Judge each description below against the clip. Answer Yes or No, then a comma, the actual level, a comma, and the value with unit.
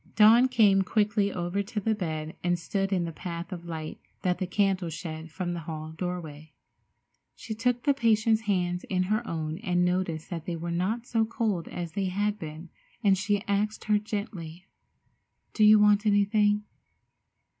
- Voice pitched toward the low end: No, high, 190 Hz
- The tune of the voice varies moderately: Yes, average, 3.7 semitones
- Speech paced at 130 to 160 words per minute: No, average, 170 wpm